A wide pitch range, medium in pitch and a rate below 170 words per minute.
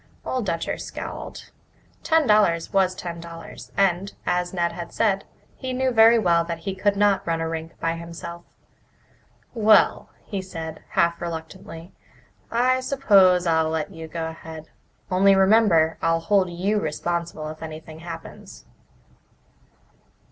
No: average, 3.3 semitones; medium, 175 Hz; average, 140 wpm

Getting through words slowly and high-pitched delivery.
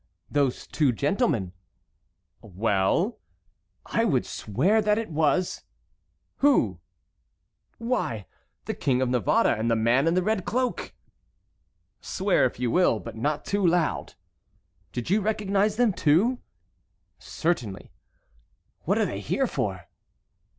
No: slow, 120 wpm; medium, 160 Hz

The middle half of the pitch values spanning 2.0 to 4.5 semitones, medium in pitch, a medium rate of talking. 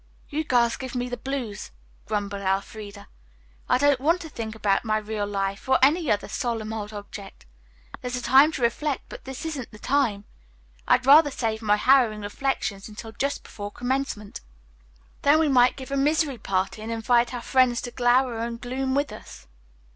No: average, 4.2 semitones; high, 240 Hz; average, 185 wpm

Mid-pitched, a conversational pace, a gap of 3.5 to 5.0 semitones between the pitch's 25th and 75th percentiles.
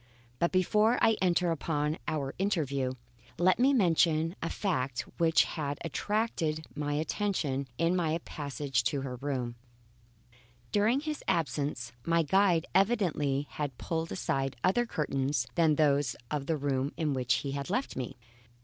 Yes: medium, 155 Hz; average, 145 wpm; average, 4.6 semitones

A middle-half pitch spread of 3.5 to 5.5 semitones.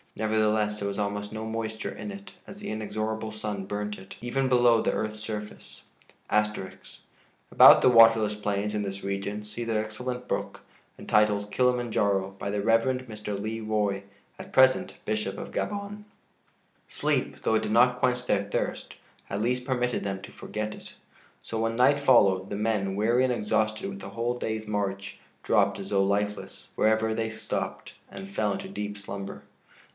No: narrow, 2.6 semitones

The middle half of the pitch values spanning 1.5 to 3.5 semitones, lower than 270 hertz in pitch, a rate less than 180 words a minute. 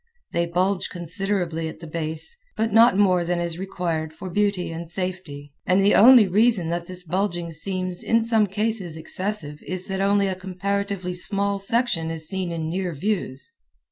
Yes: average, 3.0 semitones; medium, 185 Hz; average, 170 wpm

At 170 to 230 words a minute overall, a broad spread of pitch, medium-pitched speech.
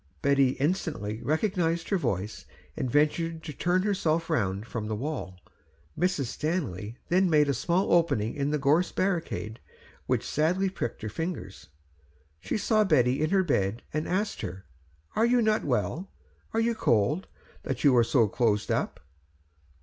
No: average, 155 wpm; wide, 7.6 semitones; medium, 150 Hz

